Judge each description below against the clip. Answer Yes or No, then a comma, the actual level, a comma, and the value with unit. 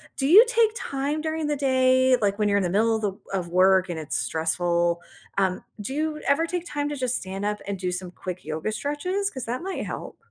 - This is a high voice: Yes, very high, 250 Hz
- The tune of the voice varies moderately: No, wide, 7.7 semitones